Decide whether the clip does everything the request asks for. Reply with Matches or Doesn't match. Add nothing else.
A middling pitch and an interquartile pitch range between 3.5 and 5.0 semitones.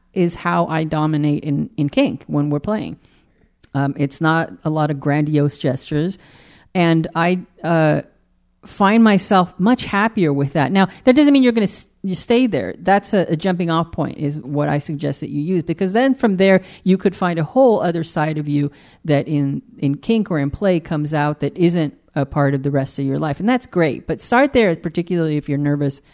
Matches